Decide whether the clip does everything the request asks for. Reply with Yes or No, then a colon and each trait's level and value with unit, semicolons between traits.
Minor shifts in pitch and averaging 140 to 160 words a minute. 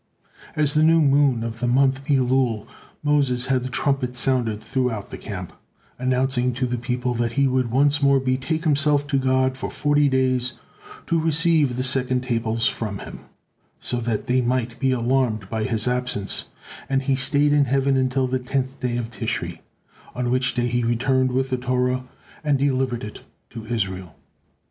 No: narrow, 2.0 semitones; average, 175 wpm